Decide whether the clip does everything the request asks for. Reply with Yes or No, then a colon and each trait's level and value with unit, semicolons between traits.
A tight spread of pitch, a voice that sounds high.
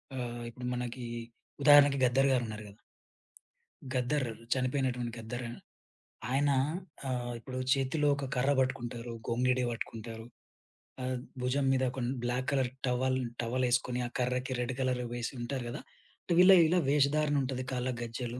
No: narrow, 1.6 semitones; low, 125 Hz